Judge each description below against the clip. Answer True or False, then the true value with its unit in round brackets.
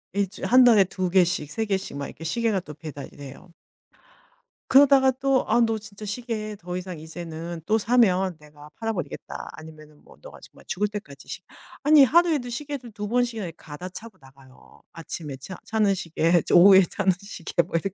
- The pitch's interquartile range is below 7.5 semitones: True (5.6 semitones)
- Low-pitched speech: False (195 Hz)